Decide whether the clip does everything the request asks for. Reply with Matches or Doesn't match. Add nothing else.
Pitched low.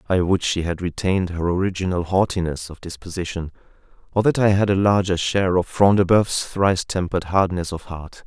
Matches